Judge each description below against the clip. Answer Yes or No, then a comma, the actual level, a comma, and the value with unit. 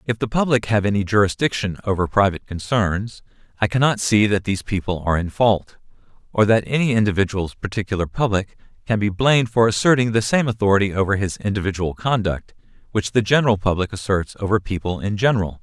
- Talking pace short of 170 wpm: No, average, 175 wpm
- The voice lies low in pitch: Yes, low, 105 Hz